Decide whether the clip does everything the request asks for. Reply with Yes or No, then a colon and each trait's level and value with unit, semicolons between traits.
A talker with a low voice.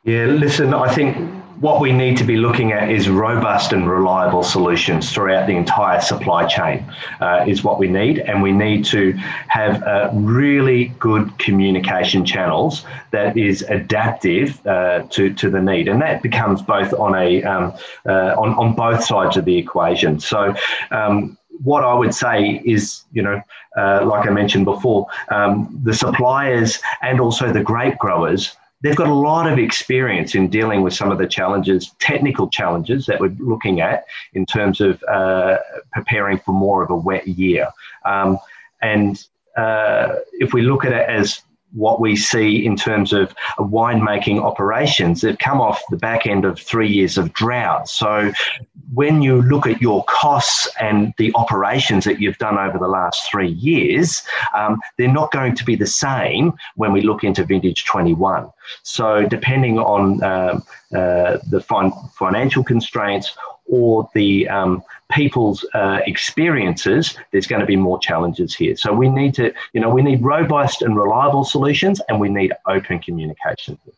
Yes: low, 105 Hz